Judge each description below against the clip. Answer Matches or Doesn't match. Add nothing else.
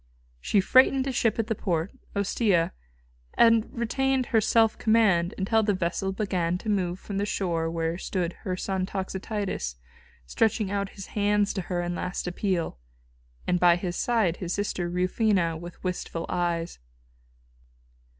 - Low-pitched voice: Doesn't match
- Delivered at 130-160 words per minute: Matches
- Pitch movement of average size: Matches